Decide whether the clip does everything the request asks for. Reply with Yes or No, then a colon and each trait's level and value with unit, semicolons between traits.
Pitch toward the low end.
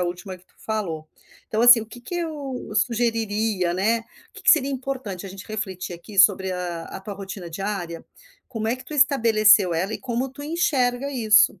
No: high, 215 Hz